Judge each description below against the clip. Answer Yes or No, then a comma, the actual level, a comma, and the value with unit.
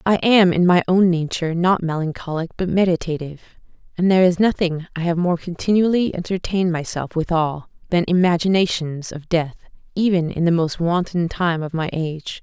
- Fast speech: No, average, 165 wpm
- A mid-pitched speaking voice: Yes, medium, 175 Hz